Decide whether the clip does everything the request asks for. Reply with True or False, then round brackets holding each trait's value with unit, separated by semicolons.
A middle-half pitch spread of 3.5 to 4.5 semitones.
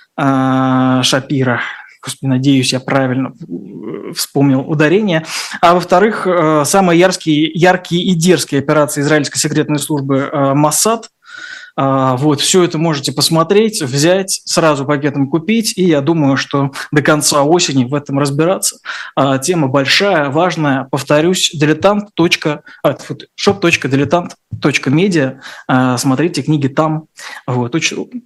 True (4.0 semitones)